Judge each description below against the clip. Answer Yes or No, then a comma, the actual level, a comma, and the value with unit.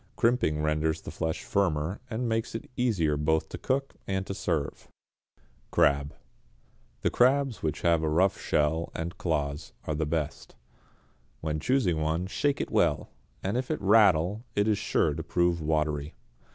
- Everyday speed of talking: Yes, average, 155 wpm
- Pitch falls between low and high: No, very low, 85 Hz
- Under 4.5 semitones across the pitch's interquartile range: No, wide, 5.6 semitones